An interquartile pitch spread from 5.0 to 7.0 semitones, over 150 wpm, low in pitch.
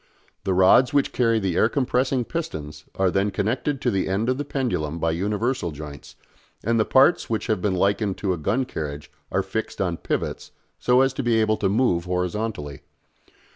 Yes: wide, 5.5 semitones; average, 190 wpm; low, 105 Hz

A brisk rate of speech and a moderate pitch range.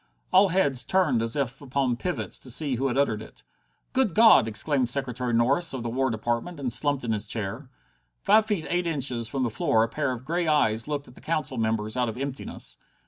Yes: fast, 215 wpm; average, 4.5 semitones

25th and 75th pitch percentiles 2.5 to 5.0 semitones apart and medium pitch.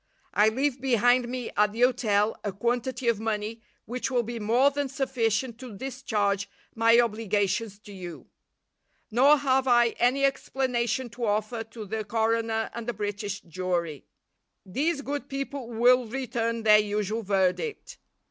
No: average, 3.3 semitones; high, 230 Hz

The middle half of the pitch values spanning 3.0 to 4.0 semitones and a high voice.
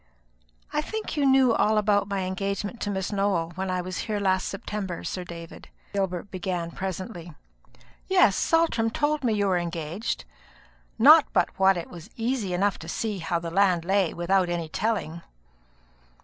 Yes: average, 3.5 semitones; high, 195 Hz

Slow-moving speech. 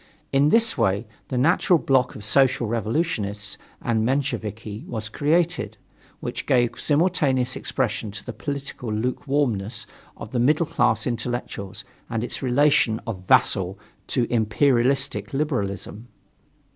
Yes: slow, 120 wpm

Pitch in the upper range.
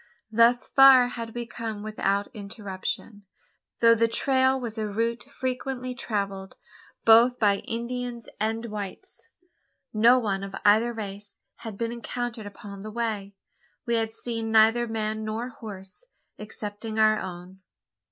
Yes: high, 225 Hz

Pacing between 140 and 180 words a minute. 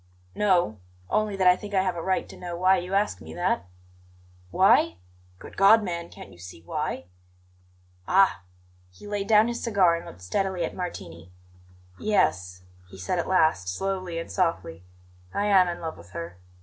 Yes: average, 175 wpm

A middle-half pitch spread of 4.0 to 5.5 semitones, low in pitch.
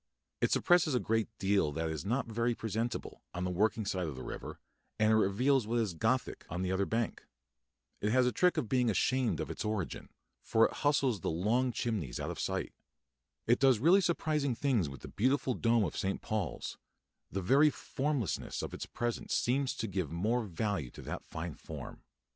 Yes: average, 5.1 semitones; low, 110 Hz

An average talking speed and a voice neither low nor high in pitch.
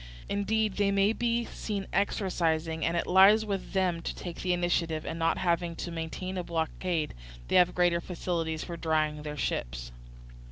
Yes: average, 170 wpm; medium, 175 Hz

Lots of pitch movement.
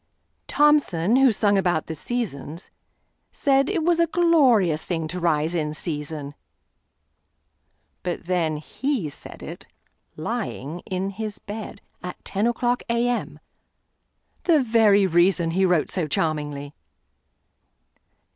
Yes: wide, 7.0 semitones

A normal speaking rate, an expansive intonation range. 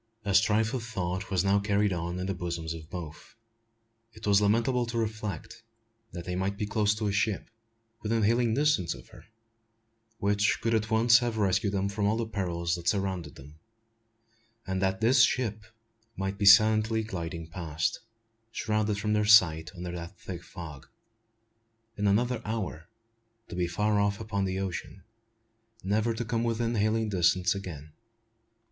No: average, 165 wpm; average, 3.5 semitones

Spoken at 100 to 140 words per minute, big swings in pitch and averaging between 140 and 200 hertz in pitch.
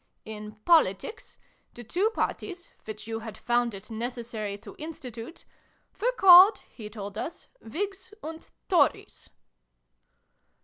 No: slow, 135 wpm; wide, 8.4 semitones; high, 240 Hz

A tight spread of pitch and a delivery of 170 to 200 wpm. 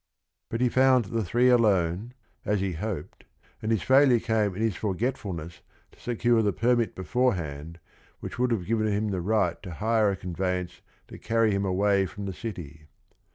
No: average, 4.0 semitones; average, 175 wpm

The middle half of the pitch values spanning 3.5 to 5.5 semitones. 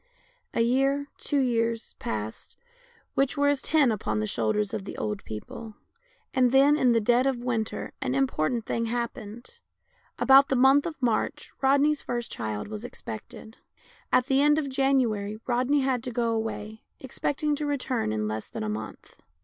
Yes: average, 4.0 semitones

